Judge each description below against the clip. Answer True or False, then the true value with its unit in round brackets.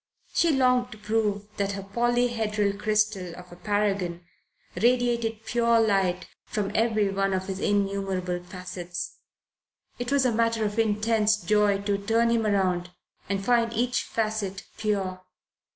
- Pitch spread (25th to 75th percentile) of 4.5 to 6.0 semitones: False (2.7 semitones)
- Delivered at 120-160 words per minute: True (140 wpm)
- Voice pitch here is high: True (210 Hz)